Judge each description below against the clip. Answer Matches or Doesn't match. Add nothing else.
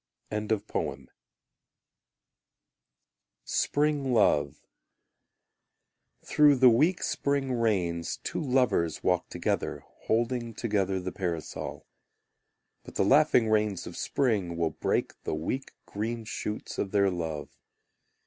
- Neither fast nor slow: Doesn't match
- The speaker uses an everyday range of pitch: Doesn't match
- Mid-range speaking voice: Doesn't match